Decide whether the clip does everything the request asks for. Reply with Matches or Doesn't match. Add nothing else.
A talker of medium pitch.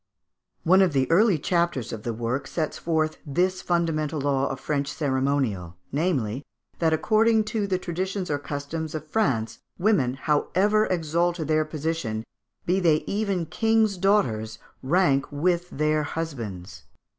Matches